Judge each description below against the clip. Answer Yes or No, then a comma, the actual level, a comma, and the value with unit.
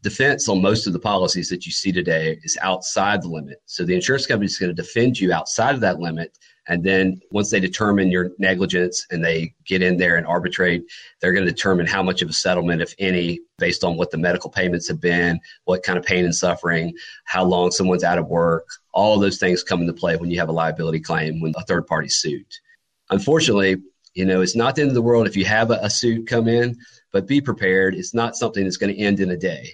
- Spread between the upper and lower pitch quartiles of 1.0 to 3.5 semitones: Yes, average, 3.1 semitones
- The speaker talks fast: Yes, fast, 245 wpm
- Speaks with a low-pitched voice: Yes, very low, 95 Hz